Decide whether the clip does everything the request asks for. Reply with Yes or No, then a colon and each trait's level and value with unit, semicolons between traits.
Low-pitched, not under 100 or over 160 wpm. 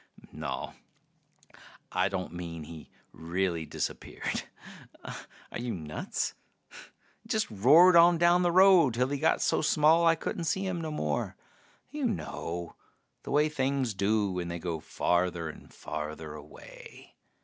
Yes: low, 110 Hz; average, 140 wpm